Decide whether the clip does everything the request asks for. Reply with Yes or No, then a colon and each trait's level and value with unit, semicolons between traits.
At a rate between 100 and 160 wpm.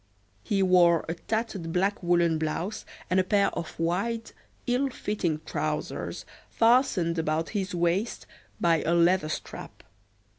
Yes: slow, 135 wpm